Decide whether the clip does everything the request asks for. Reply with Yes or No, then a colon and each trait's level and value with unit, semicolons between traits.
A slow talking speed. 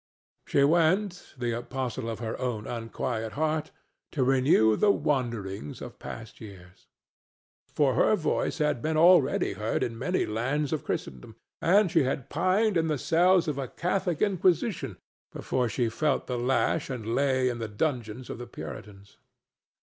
No: average, 155 wpm